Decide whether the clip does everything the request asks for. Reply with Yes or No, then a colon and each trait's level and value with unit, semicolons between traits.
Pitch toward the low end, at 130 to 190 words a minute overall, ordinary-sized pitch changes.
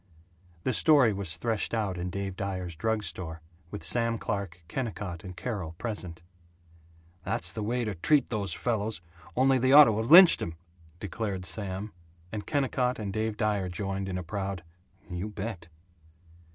Yes: low, 100 Hz; average, 160 wpm; average, 3.8 semitones